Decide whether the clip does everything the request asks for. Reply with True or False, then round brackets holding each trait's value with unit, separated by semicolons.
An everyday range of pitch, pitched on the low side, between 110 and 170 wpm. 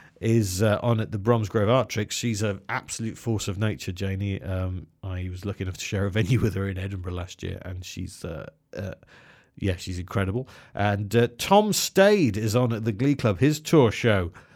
False (3.6 semitones; 105 Hz; 205 wpm)